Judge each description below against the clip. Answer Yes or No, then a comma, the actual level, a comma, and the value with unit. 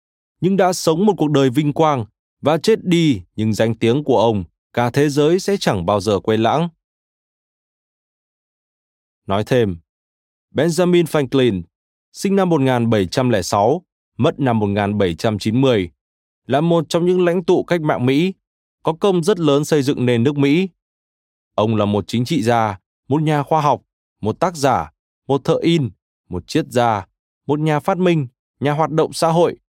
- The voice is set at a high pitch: No, low, 135 Hz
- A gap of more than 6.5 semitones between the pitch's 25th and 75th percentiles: Yes, wide, 7.8 semitones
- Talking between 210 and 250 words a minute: No, slow, 165 wpm